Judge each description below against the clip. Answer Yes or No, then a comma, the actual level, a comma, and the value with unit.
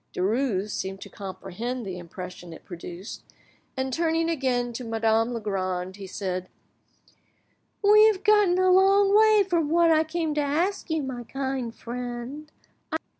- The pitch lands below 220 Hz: No, very high, 255 Hz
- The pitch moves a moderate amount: No, wide, 8.8 semitones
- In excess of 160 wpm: No, average, 145 wpm